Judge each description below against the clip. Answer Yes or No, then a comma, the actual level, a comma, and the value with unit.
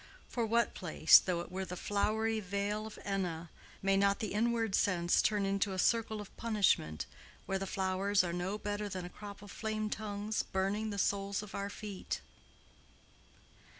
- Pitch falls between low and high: No, high, 200 Hz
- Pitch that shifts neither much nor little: No, narrow, 2.0 semitones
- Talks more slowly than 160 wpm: No, average, 175 wpm